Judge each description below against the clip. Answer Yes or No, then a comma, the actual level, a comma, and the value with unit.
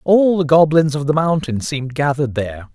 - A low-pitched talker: No, medium, 145 Hz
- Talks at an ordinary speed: Yes, average, 195 wpm